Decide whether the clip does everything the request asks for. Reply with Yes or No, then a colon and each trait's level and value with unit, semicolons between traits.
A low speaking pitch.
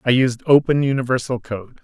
Yes: low, 130 Hz